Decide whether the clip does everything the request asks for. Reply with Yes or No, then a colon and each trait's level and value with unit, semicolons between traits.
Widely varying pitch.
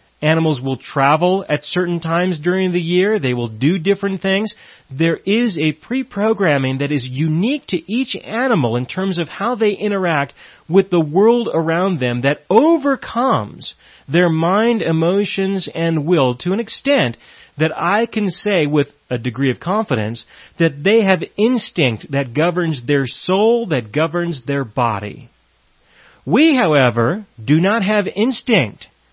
Yes: wide, 6.2 semitones